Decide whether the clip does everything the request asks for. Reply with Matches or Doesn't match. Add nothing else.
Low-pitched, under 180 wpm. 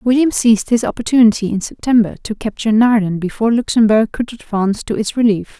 Doesn't match